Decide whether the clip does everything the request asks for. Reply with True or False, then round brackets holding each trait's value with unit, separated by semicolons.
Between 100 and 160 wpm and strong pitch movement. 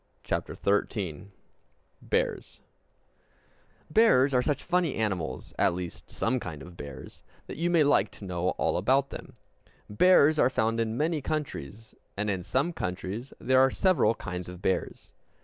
True (150 wpm; 7.8 semitones)